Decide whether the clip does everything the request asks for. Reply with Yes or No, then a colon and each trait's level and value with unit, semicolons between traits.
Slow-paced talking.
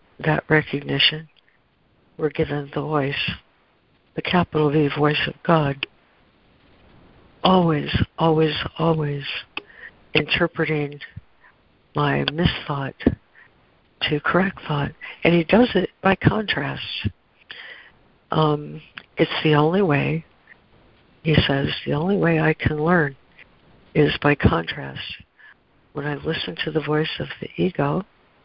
Yes: slow, 110 wpm